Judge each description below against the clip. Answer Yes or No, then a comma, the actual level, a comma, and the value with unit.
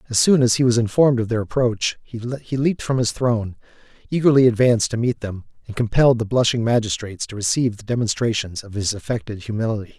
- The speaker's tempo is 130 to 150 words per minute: No, average, 190 wpm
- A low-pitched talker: Yes, low, 115 Hz